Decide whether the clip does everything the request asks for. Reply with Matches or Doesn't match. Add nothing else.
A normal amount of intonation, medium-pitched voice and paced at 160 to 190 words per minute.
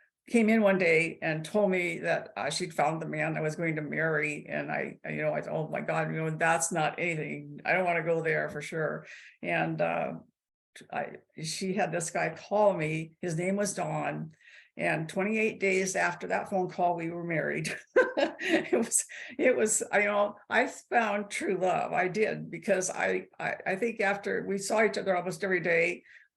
Doesn't match